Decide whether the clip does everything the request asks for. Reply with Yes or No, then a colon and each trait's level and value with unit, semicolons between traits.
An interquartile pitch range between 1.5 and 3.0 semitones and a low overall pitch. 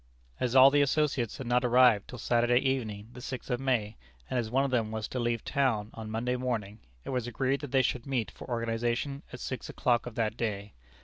Yes: narrow, 2.4 semitones; low, 120 Hz